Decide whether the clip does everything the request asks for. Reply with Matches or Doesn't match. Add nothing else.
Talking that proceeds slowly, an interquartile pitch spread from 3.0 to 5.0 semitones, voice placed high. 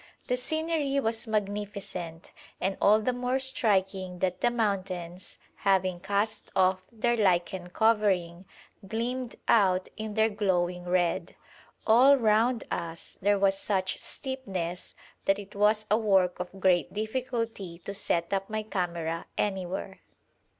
Matches